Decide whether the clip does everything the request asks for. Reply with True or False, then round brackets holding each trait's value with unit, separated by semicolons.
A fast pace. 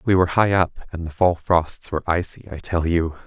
True (240 wpm)